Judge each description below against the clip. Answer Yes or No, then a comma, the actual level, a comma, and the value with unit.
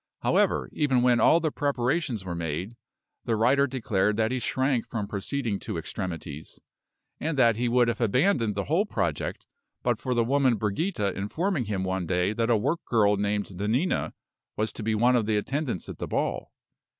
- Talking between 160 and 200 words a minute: Yes, average, 185 wpm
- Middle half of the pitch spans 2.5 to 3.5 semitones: No, average, 4.5 semitones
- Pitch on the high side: No, low, 115 Hz